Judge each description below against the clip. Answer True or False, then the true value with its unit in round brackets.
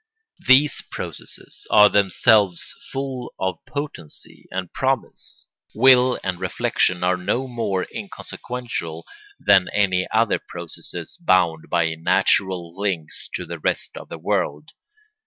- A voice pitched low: True (95 Hz)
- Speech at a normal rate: False (120 wpm)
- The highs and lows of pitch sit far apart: True (5.8 semitones)